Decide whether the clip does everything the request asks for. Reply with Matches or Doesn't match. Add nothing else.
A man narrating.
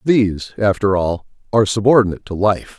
Matches